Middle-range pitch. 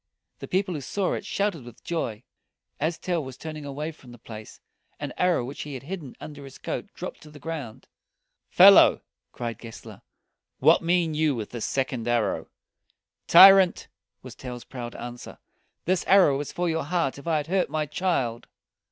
Yes: medium, 150 Hz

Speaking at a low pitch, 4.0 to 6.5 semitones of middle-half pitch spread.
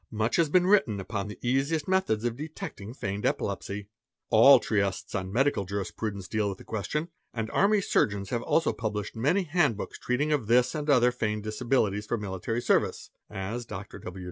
Yes: low, 115 Hz; wide, 5.6 semitones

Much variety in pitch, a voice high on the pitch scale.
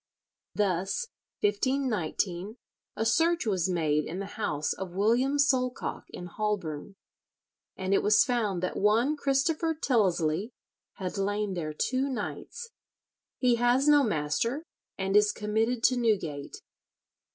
Yes: wide, 5.7 semitones; high, 210 Hz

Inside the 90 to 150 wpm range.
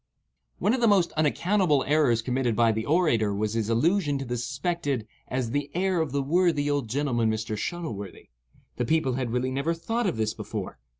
No: average, 190 wpm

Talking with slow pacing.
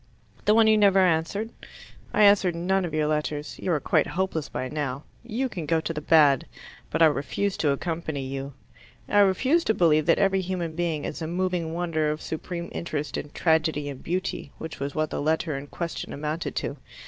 No: average, 200 wpm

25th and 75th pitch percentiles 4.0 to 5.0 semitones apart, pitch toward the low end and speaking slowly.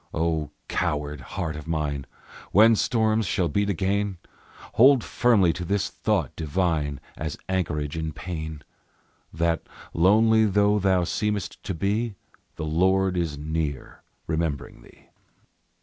Yes: average, 4.5 semitones; very low, 85 Hz; slow, 125 wpm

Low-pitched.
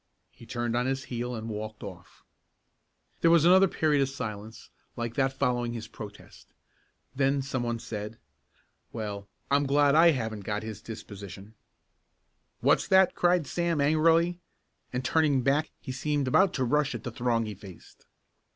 Yes: low, 125 Hz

